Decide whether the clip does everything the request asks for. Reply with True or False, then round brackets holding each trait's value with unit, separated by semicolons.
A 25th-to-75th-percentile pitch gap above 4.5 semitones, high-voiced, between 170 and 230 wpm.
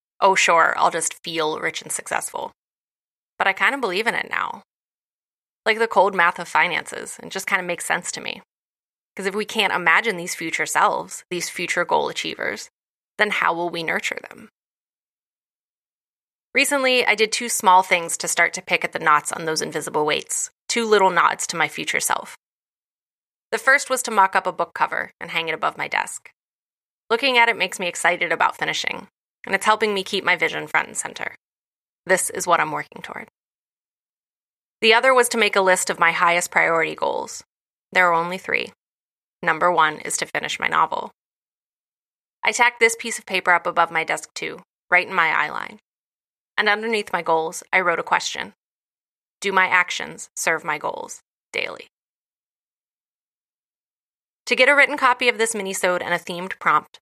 True (5.1 semitones; 195 Hz; 185 wpm)